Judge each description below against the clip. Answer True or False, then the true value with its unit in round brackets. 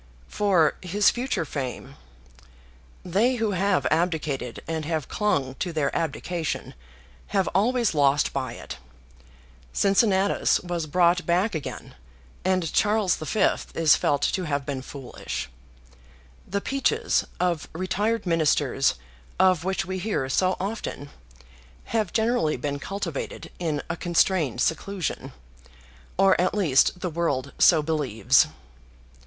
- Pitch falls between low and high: True (175 Hz)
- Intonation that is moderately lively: True (4.8 semitones)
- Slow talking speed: True (120 wpm)